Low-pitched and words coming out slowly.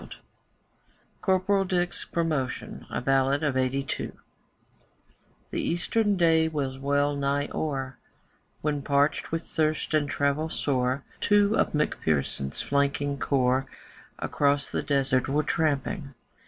No: medium, 145 Hz; slow, 115 wpm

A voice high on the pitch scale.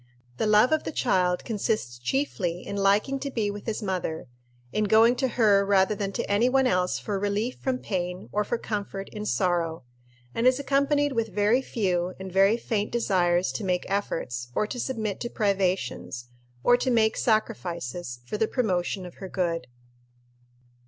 Yes: high, 205 Hz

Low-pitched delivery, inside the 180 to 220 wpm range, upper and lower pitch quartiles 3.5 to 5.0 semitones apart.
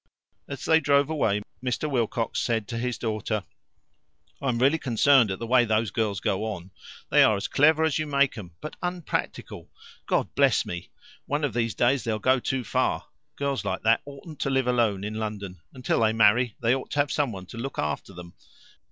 Yes: low, 120 Hz; average, 200 wpm; average, 4.4 semitones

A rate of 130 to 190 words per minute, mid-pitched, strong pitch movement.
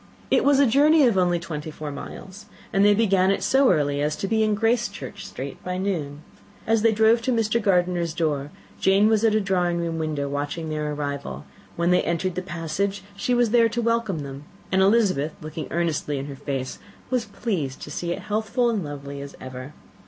No: fast, 205 wpm; medium, 180 Hz; wide, 6.5 semitones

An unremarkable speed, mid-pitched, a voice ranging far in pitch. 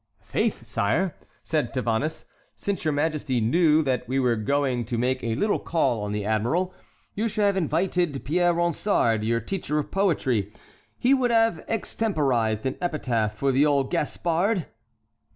Yes: average, 155 wpm; medium, 145 Hz; wide, 6.9 semitones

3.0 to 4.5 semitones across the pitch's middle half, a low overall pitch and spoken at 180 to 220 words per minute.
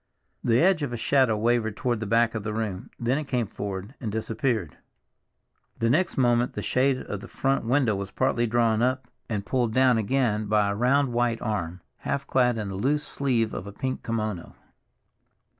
Yes: average, 3.3 semitones; low, 115 Hz; average, 190 wpm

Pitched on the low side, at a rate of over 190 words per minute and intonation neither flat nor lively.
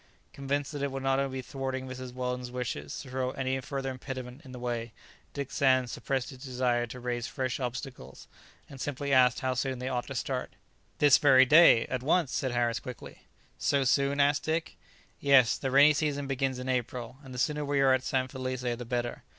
No: low, 130 Hz; average, 200 wpm; narrow, 1.7 semitones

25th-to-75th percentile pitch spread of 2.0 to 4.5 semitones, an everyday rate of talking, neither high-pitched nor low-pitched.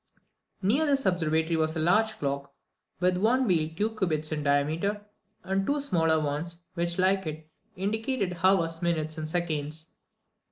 Yes: average, 3.9 semitones; average, 150 wpm; medium, 170 Hz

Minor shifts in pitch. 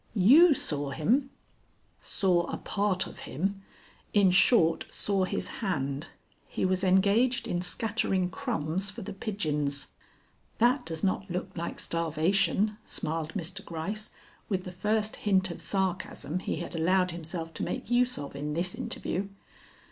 No: average, 4.0 semitones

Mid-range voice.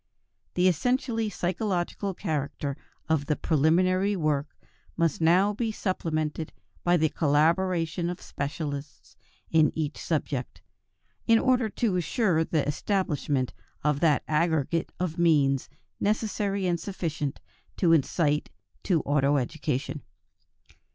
Yes: medium, 165 Hz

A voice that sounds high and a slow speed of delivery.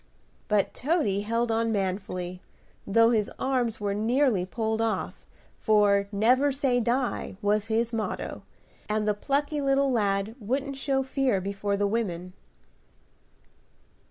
Yes: high, 225 Hz; slow, 130 wpm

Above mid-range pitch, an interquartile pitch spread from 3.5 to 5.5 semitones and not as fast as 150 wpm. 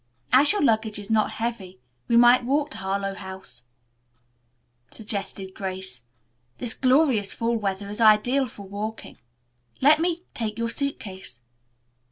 Yes: high, 220 Hz; average, 4.1 semitones; average, 140 wpm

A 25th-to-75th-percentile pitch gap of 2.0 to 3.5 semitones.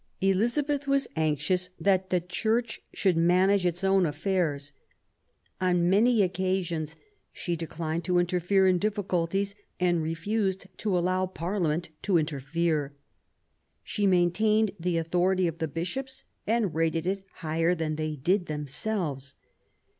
Yes: average, 3.0 semitones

